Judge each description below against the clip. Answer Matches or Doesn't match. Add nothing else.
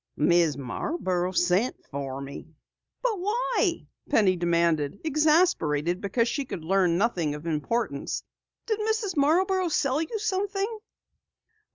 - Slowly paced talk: Matches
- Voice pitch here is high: Matches